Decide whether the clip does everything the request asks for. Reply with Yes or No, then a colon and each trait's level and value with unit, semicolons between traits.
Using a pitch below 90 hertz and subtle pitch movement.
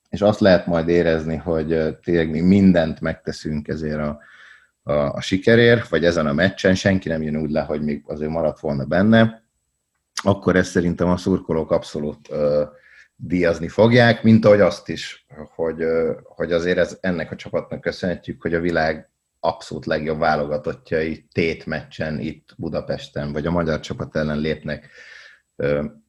No: very low, 80 Hz; average, 3.0 semitones